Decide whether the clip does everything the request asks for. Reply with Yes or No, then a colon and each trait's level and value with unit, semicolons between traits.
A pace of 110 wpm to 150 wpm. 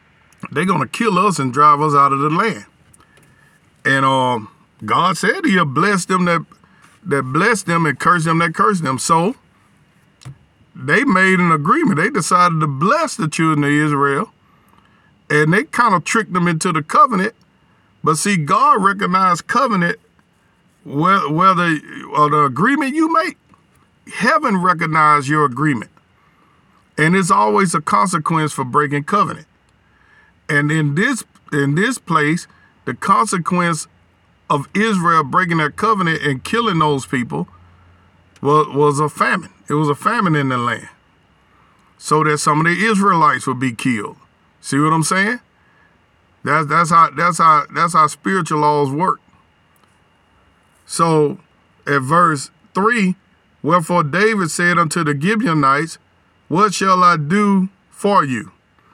Yes: average, 145 wpm